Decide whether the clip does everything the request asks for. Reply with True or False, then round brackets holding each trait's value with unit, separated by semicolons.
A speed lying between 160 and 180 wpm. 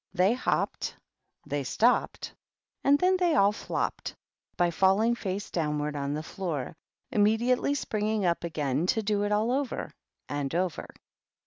False (145 wpm)